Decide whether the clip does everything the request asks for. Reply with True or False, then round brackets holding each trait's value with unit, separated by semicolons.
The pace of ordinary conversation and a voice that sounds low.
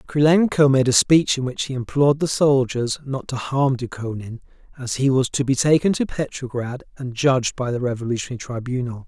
True (185 wpm; 130 Hz)